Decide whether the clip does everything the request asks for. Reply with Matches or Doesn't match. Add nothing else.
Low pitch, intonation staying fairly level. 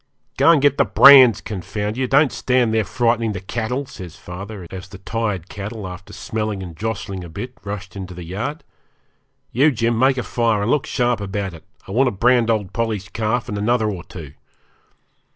Doesn't match